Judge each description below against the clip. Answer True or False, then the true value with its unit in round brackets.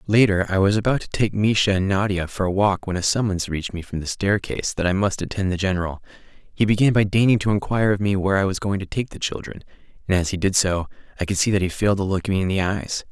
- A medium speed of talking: False (270 wpm)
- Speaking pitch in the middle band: False (100 Hz)